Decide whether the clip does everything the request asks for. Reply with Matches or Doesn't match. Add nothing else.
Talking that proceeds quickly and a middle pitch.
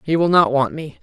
Matches